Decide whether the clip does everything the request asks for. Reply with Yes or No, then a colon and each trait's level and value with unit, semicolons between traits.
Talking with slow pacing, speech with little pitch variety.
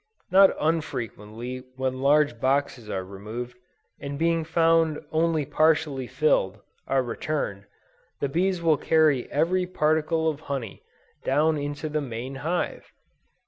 No: slow, 125 wpm; average, 3.9 semitones